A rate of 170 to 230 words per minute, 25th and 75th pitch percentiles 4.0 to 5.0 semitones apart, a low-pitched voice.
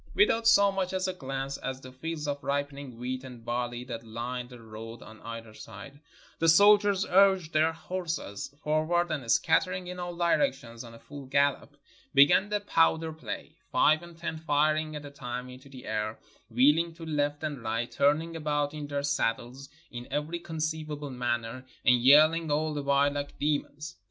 No: average, 175 wpm; average, 4.4 semitones; medium, 145 Hz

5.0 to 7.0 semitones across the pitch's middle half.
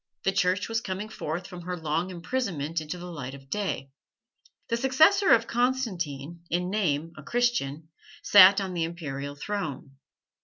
Yes: average, 5.3 semitones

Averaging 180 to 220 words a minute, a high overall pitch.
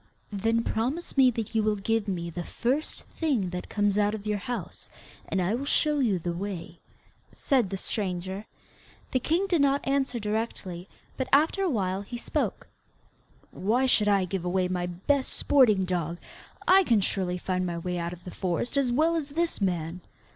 Yes: average, 185 wpm; high, 210 Hz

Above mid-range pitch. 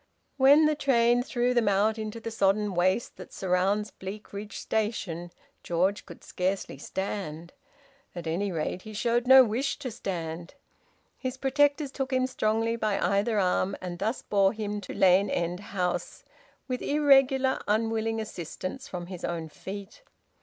Yes: high, 210 Hz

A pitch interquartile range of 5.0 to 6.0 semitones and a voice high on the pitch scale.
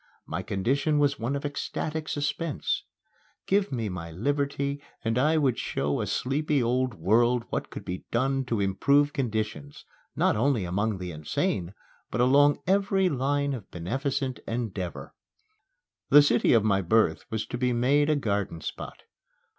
No: wide, 5.5 semitones; low, 125 Hz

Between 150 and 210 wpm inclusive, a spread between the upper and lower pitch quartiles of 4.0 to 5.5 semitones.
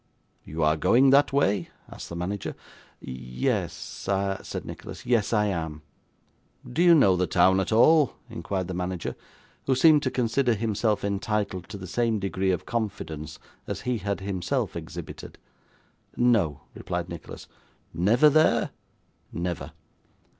No: average, 140 wpm; average, 5.1 semitones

